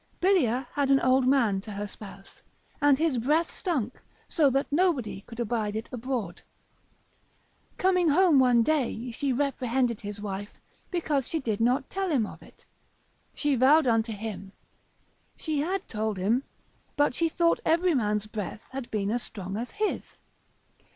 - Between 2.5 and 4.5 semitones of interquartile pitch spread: No, average, 5.3 semitones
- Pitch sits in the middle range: No, very high, 255 Hz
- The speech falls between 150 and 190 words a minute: Yes, average, 155 wpm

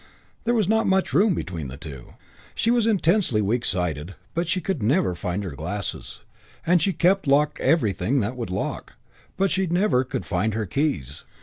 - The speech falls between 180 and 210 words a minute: Yes, average, 185 wpm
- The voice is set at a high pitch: No, low, 130 Hz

